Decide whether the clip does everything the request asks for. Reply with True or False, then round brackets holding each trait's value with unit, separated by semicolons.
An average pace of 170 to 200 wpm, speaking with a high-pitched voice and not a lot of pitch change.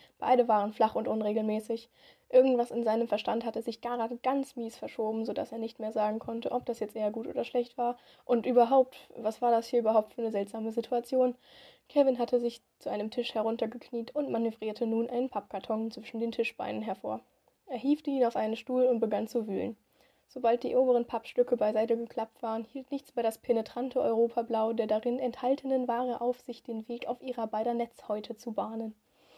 True (190 wpm; 235 Hz; 1.8 semitones)